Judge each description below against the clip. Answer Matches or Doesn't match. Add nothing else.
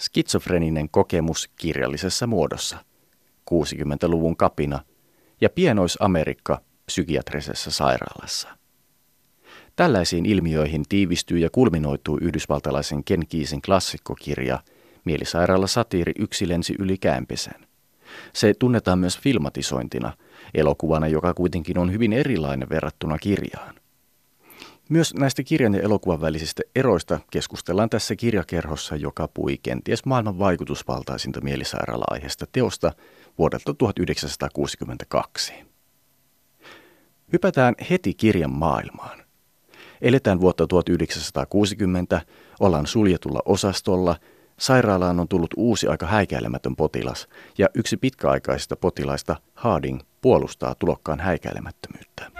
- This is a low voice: Matches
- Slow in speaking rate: Matches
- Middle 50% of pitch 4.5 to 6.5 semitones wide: Matches